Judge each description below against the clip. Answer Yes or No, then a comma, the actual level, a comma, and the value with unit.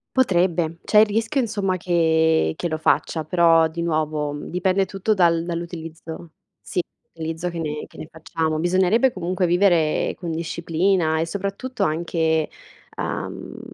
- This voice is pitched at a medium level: Yes, medium, 170 Hz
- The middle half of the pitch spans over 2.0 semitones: Yes, narrow, 2.6 semitones